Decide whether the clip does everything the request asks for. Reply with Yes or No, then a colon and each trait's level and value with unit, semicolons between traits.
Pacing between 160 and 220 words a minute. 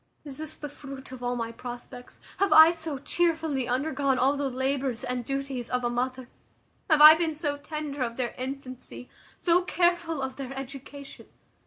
Yes: average, 175 wpm